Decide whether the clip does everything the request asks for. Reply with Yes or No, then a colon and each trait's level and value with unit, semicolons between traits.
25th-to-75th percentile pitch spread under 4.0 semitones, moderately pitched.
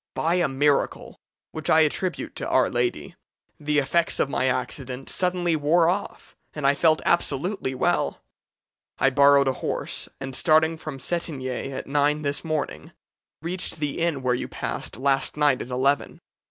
Yes: average, 3.3 semitones; medium, 145 Hz